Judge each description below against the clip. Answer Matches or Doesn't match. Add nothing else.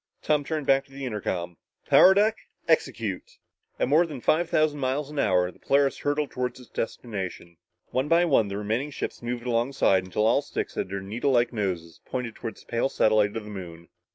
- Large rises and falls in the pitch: Matches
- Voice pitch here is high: Doesn't match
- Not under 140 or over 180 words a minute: Doesn't match